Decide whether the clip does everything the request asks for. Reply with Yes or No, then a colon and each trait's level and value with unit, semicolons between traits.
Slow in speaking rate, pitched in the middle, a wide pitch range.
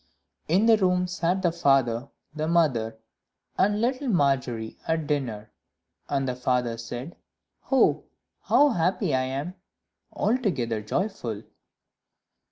Yes: slow, 115 wpm; medium, 150 Hz; wide, 7.2 semitones